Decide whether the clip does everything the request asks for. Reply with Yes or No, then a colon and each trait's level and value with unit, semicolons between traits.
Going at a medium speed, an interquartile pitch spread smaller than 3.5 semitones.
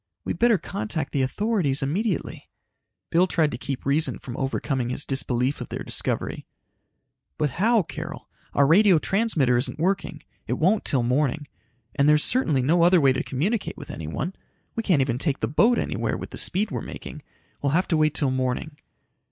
No: average, 180 wpm; wide, 5.4 semitones